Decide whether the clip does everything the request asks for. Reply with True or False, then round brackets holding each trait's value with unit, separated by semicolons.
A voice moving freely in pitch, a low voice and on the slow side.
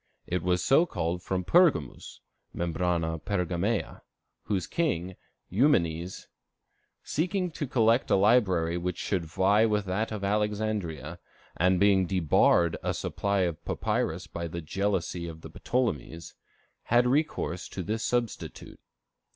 False (4.4 semitones; 95 Hz; 125 wpm)